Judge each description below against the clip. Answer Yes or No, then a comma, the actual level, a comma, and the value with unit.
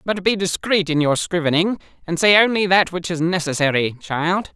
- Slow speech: No, average, 185 wpm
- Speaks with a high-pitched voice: No, medium, 175 Hz